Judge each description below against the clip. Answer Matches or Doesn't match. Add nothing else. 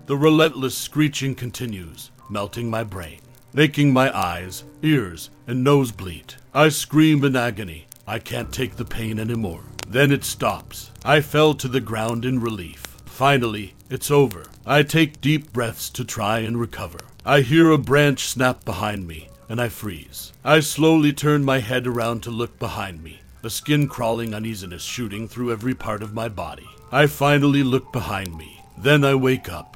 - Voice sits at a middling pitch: Doesn't match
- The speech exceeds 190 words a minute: Doesn't match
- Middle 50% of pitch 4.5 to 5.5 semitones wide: Matches